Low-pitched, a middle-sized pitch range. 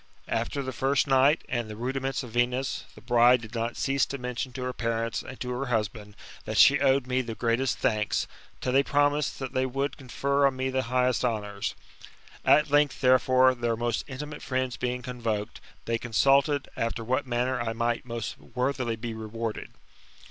No: low, 125 Hz; narrow, 2.3 semitones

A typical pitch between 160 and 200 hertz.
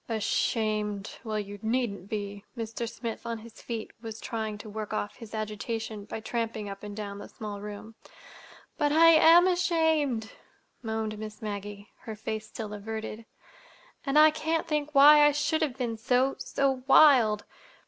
No: high, 225 Hz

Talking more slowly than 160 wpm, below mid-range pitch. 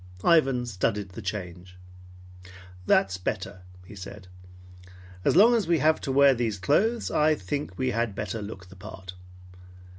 Yes: average, 150 wpm; low, 105 Hz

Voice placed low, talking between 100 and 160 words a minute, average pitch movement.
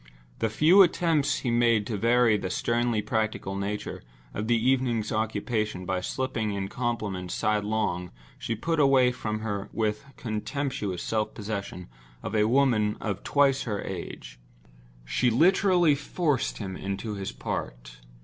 Yes: low, 110 Hz; average, 145 wpm; average, 3.9 semitones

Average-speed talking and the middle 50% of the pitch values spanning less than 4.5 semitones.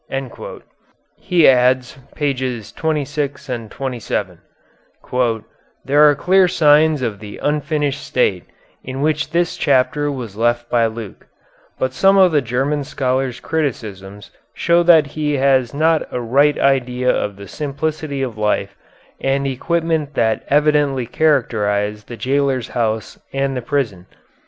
No: slow, 130 wpm; average, 3.9 semitones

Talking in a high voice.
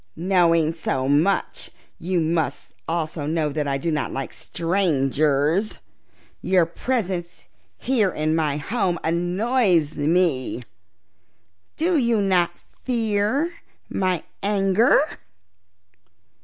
No: medium, 175 Hz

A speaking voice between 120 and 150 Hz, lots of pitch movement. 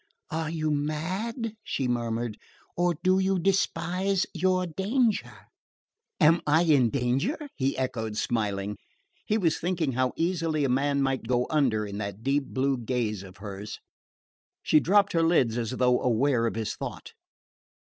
Yes: medium, 140 Hz; wide, 6.7 semitones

